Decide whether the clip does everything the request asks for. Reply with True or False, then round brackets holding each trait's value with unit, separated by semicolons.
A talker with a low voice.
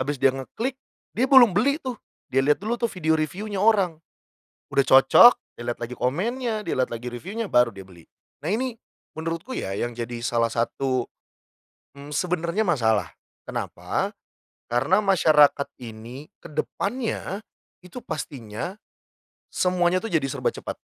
False (160 Hz)